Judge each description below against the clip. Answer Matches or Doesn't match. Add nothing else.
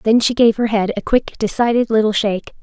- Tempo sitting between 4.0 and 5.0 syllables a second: Doesn't match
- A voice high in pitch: Matches